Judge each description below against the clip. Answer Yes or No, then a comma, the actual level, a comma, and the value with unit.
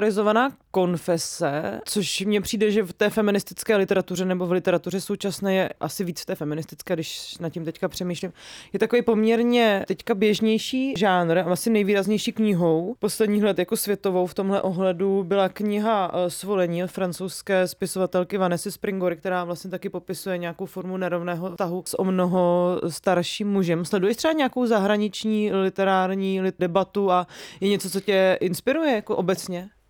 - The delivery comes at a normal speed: Yes, average, 155 wpm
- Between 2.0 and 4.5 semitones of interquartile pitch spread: Yes, narrow, 2.5 semitones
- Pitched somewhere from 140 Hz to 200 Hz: Yes, high, 190 Hz